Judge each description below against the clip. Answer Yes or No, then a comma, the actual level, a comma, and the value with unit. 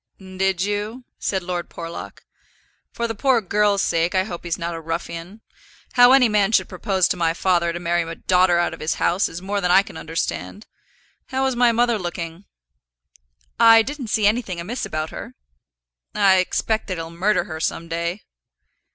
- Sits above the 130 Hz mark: Yes, medium, 185 Hz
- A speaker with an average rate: Yes, average, 185 wpm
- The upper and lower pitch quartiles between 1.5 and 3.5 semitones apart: No, average, 4.0 semitones